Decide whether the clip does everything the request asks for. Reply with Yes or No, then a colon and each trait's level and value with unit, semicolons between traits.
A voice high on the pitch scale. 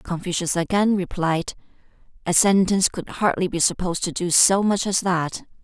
No: medium, 180 Hz